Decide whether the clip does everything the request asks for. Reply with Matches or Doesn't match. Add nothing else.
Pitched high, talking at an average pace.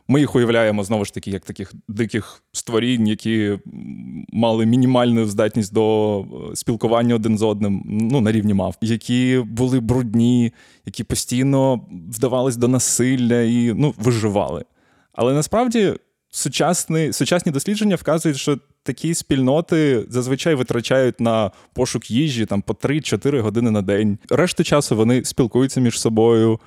Doesn't match